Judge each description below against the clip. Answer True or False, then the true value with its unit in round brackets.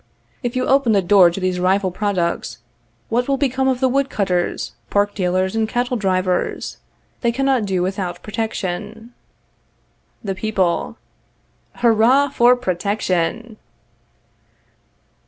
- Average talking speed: False (120 wpm)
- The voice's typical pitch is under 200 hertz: False (210 Hz)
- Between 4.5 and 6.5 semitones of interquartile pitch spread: True (4.8 semitones)